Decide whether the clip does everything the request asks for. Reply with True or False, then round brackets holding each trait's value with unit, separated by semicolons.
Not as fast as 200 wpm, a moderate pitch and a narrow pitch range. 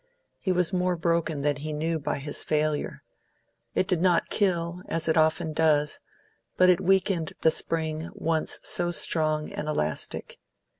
True (155 wpm; 160 Hz; 2.3 semitones)